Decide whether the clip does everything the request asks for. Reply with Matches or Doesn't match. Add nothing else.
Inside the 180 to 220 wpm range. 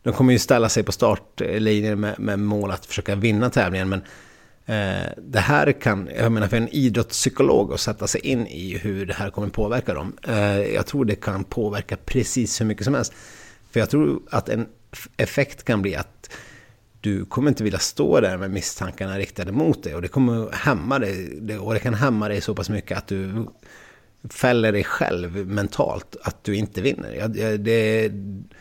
Matches